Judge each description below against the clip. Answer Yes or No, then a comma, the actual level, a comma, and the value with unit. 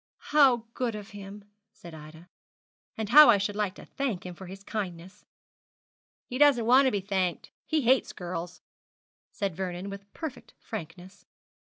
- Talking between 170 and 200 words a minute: No, average, 160 wpm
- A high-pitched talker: Yes, high, 200 Hz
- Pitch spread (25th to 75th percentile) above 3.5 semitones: Yes, average, 4.6 semitones